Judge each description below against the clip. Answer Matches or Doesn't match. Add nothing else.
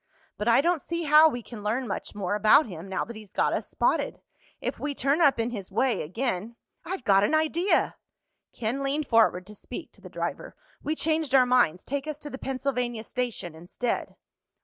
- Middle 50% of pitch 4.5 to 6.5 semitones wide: Matches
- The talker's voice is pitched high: Matches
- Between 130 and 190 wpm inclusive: Doesn't match